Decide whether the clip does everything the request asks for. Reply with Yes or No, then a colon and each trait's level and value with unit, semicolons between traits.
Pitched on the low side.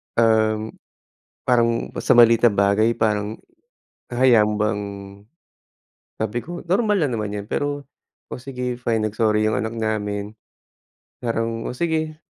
Yes: low, 115 Hz